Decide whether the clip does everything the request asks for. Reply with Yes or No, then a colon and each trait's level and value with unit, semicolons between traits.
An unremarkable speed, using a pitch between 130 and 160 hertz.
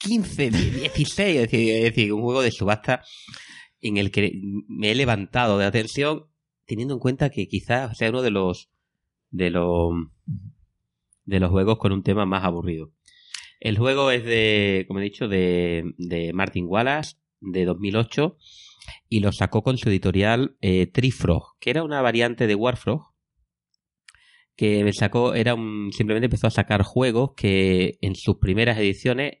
No: average, 160 wpm; low, 105 Hz